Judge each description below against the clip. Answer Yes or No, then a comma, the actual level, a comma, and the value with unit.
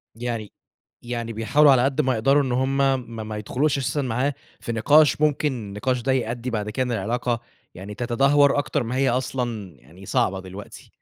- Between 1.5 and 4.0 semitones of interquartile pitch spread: Yes, average, 3.4 semitones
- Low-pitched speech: Yes, low, 125 Hz